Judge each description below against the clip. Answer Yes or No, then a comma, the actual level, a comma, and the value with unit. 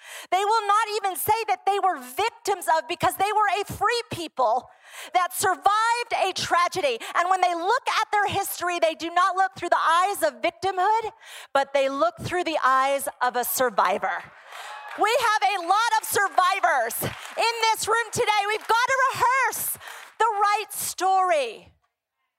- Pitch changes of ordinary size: Yes, average, 3.7 semitones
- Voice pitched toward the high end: Yes, very high, 385 Hz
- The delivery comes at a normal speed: Yes, average, 165 wpm